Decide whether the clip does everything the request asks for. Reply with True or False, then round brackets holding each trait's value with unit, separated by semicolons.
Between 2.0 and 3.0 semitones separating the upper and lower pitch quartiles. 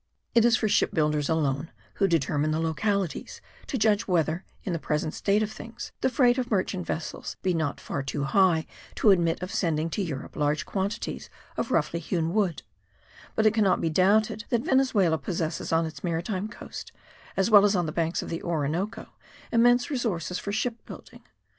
False (5.1 semitones)